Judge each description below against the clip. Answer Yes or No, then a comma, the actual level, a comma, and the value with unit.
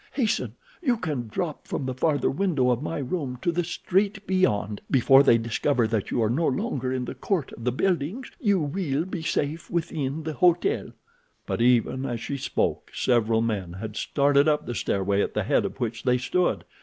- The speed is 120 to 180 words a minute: No, average, 195 wpm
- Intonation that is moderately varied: No, wide, 6.1 semitones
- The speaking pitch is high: No, medium, 140 Hz